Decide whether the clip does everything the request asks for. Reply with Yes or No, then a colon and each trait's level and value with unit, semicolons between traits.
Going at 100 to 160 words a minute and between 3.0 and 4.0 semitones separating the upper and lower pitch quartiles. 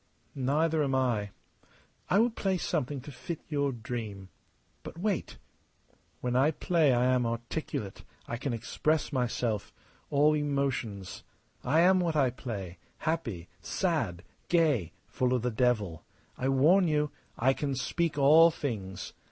No: average, 140 wpm; average, 5.0 semitones